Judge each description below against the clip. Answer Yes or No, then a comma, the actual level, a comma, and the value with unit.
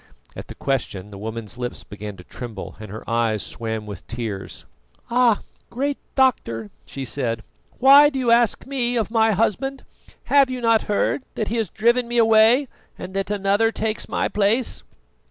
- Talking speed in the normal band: Yes, average, 170 wpm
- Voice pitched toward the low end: No, high, 210 Hz